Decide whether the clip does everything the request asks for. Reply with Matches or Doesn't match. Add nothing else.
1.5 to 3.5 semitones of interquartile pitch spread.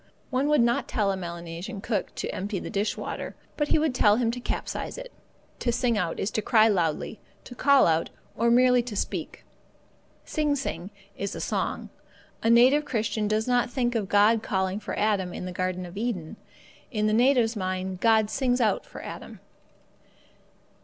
Doesn't match